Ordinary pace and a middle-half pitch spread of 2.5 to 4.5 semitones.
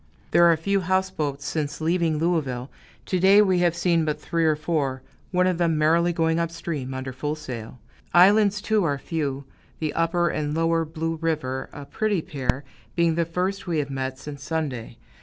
Yes: average, 185 wpm; average, 3.2 semitones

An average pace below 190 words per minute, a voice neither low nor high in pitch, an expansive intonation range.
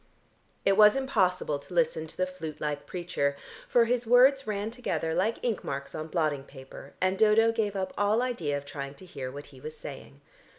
No: average, 200 wpm; medium, 180 Hz; wide, 7.2 semitones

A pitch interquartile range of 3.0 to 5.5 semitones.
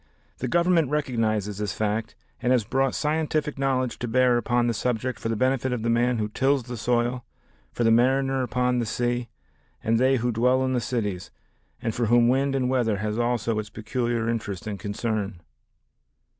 No: narrow, 2.5 semitones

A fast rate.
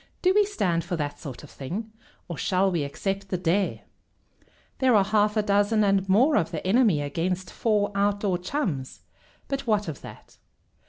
No: average, 175 wpm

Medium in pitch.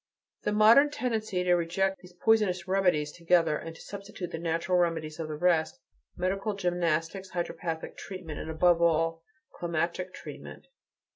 Yes: medium, 175 Hz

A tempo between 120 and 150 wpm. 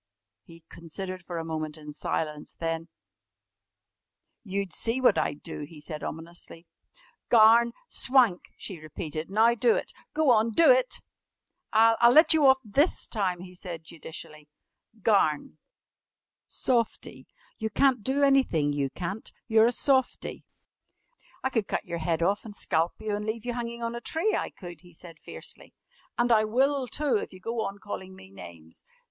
No: average, 165 wpm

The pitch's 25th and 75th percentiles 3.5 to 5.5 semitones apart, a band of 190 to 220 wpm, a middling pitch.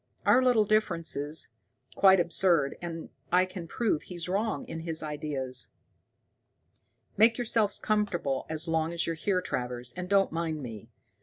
No: average, 4.4 semitones; average, 145 wpm; medium, 170 Hz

